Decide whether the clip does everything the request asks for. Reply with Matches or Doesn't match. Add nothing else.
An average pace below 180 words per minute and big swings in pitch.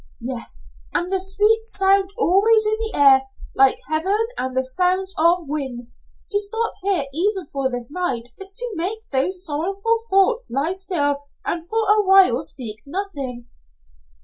Matches